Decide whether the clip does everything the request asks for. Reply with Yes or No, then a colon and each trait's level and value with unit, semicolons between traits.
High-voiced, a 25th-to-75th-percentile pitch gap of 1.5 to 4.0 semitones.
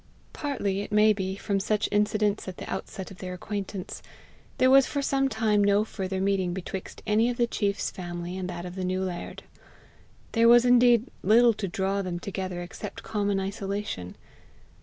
Yes: high, 200 Hz; narrow, 2.6 semitones